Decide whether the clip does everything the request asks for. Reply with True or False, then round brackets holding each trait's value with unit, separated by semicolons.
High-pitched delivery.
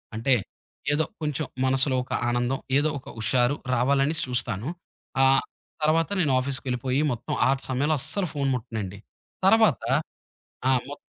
False (135 Hz)